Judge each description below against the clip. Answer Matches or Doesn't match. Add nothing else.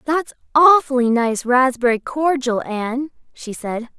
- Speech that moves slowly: Matches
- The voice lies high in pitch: Matches